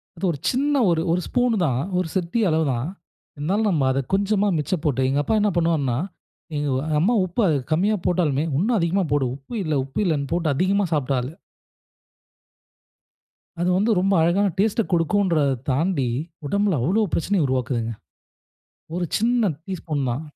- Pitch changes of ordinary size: No, wide, 6.0 semitones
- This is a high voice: No, medium, 170 Hz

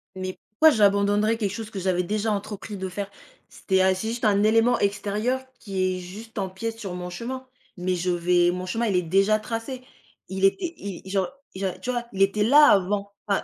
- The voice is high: Yes, high, 200 Hz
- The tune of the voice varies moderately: Yes, average, 3.0 semitones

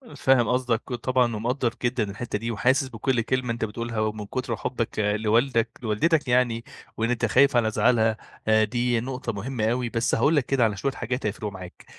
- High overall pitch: No, low, 120 Hz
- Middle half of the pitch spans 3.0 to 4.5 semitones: No, narrow, 2.4 semitones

